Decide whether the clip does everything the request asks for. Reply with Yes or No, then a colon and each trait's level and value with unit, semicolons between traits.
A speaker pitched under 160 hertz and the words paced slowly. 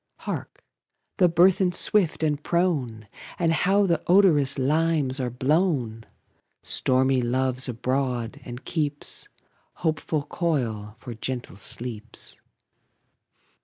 Yes: low, 135 Hz; slow, 100 wpm